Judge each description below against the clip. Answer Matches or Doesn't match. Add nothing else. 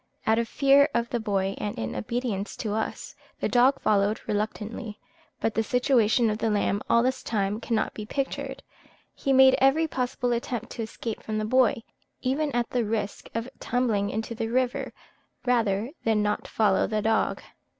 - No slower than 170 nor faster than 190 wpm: Matches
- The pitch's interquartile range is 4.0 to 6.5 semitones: Doesn't match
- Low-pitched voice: Doesn't match